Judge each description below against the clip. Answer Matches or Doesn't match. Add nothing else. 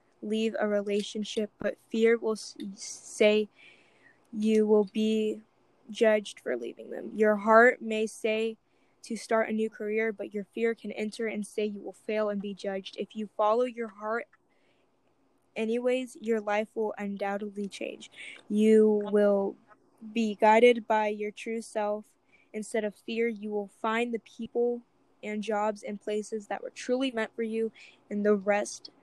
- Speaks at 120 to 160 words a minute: Matches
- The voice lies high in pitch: Matches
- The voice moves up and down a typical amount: Doesn't match